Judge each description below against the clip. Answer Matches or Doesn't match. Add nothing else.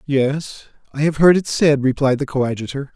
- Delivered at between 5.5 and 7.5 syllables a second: Doesn't match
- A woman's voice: Doesn't match